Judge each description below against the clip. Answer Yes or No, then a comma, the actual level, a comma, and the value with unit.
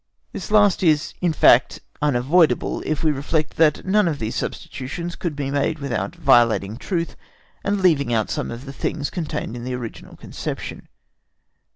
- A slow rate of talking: No, average, 165 wpm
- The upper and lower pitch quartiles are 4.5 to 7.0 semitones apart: Yes, average, 4.9 semitones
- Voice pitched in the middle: Yes, medium, 150 Hz